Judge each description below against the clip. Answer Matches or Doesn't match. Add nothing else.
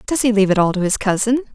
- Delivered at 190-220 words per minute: Doesn't match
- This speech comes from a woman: Matches